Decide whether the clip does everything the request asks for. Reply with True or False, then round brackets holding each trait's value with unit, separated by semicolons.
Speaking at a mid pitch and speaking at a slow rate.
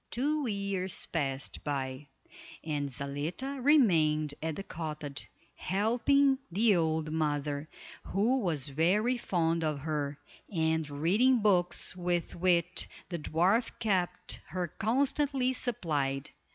True (175 Hz; 110 wpm)